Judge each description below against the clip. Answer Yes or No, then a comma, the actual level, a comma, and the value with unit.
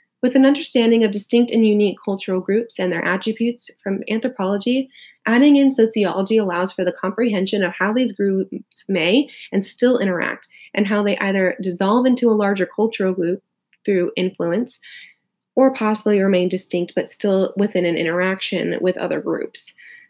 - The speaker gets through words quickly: No, average, 160 wpm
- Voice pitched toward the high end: Yes, high, 205 Hz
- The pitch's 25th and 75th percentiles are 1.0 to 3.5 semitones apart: No, average, 4.2 semitones